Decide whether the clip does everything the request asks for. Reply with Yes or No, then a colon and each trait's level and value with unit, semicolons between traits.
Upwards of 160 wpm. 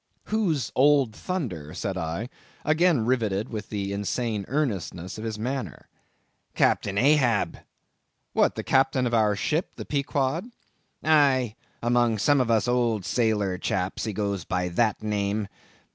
No: average, 140 wpm